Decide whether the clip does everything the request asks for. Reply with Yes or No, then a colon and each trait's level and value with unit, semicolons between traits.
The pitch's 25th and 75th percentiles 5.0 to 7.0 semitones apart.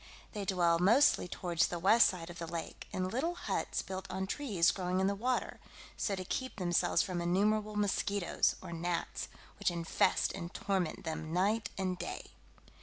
No: average, 2.9 semitones